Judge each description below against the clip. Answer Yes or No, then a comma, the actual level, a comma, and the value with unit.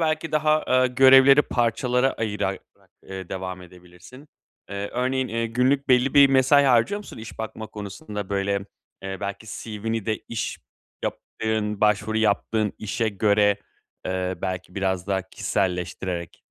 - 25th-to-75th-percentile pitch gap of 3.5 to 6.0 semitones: Yes, average, 4.7 semitones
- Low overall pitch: Yes, low, 110 Hz